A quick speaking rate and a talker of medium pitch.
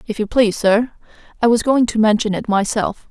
No: fast, 215 wpm; high, 220 Hz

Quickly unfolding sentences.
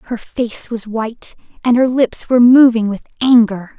No: average, 175 wpm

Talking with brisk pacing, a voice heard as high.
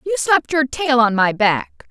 Yes: fast, 220 wpm; high, 245 Hz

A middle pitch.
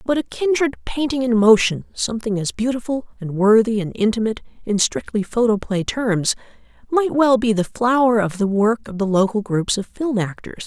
No: high, 225 Hz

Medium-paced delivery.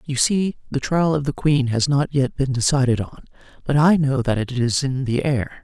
No: fast, 235 wpm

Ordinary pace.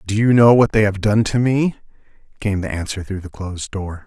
No: fast, 235 wpm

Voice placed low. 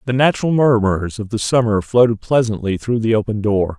Yes: low, 110 Hz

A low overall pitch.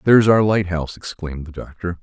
Yes: very low, 90 Hz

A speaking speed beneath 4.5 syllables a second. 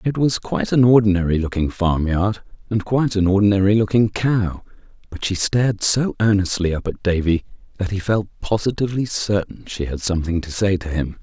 No: 5.6 syllables/s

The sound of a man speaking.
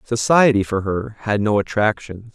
Yes: male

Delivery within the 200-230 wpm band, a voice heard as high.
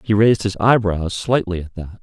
No: fast, 205 wpm; low, 100 Hz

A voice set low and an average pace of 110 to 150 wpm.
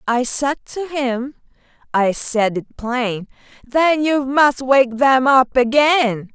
No: very high, 260 Hz; average, 140 wpm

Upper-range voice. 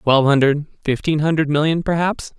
No: medium, 150 Hz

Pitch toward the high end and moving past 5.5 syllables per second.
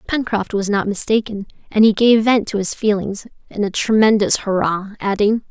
No: high, 210 Hz; 5.0 syllables/s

